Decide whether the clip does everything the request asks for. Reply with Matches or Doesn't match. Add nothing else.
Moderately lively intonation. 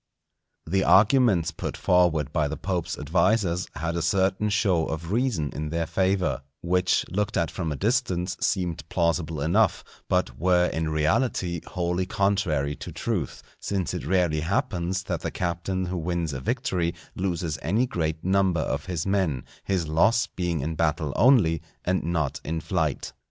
Matches